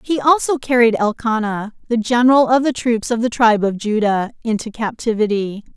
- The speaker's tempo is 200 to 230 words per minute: No, average, 165 wpm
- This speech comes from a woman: Yes, female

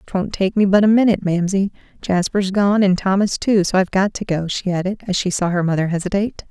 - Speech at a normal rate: No, fast, 230 wpm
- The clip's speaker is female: Yes, female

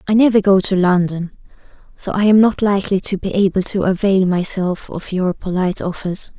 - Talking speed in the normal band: Yes, average, 190 wpm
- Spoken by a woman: Yes, female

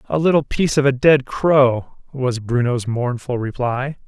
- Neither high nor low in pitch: No, low, 130 Hz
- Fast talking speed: No, average, 160 wpm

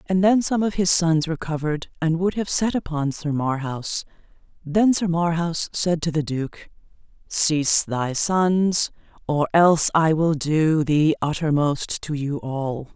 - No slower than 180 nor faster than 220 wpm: No, average, 160 wpm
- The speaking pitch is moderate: Yes, medium, 160 Hz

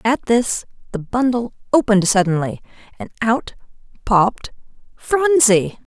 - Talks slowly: Yes, slow, 90 wpm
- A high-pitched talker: Yes, high, 230 Hz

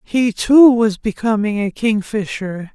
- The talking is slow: Yes, slow, 130 wpm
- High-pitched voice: Yes, high, 215 Hz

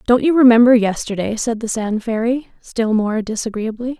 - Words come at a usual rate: Yes, average, 165 wpm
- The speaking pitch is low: No, high, 230 Hz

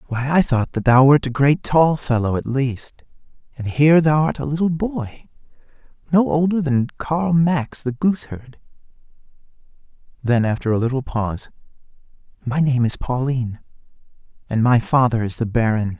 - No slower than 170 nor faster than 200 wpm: No, average, 150 wpm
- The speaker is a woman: No, male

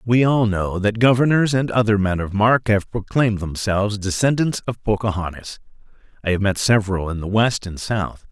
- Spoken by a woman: No, male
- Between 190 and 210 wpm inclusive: No, average, 180 wpm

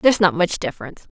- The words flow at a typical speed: No, fast, 260 wpm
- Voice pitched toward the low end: No, medium, 180 Hz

